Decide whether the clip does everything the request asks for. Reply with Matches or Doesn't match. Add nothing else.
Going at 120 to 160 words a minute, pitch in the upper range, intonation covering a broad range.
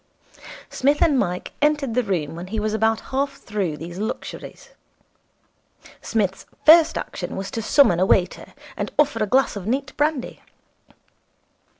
Matches